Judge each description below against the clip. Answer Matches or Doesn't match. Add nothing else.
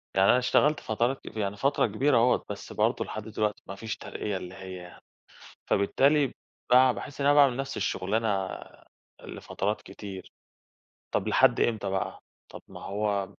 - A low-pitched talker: Matches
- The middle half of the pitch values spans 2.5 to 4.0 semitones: Doesn't match